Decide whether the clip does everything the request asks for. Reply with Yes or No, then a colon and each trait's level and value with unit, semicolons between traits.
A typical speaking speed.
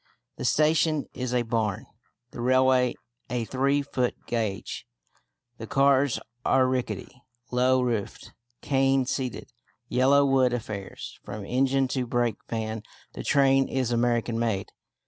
No: slow, 125 wpm